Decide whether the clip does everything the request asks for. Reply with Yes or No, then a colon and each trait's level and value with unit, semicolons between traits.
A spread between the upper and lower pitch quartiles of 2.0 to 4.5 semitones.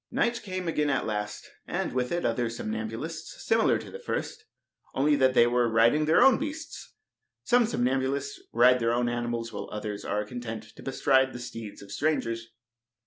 No: average, 5.1 semitones